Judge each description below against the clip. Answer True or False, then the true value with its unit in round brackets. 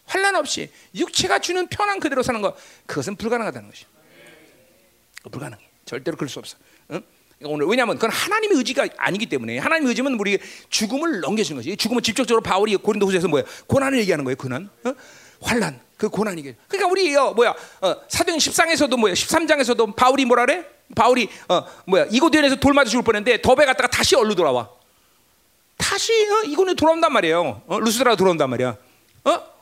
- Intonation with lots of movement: True (8.6 semitones)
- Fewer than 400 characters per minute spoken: False (425 characters per minute)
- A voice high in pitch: True (245 Hz)